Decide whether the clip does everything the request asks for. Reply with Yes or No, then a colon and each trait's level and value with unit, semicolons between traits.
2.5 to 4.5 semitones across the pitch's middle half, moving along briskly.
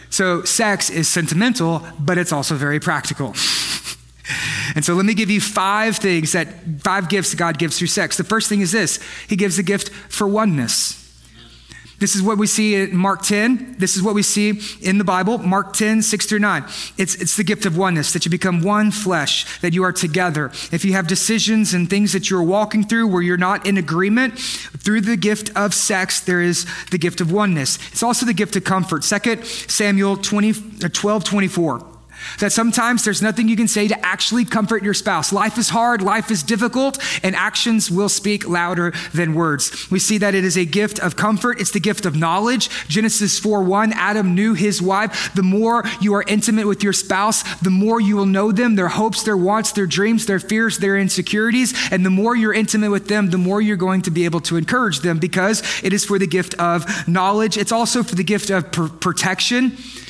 Yes: average, 3.0 semitones; fast, 210 wpm